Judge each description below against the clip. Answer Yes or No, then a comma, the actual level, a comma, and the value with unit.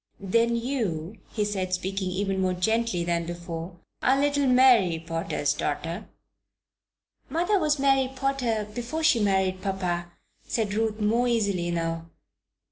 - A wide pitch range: Yes, wide, 5.8 semitones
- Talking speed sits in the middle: No, slow, 130 wpm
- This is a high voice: Yes, high, 200 Hz